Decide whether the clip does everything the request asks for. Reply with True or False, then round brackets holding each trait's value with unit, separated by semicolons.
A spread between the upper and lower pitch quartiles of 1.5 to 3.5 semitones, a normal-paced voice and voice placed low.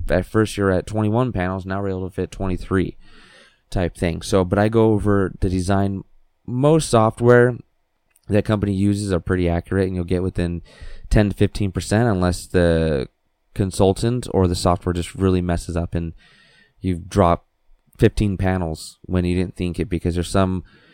True (2.6 semitones; 170 wpm; 95 Hz)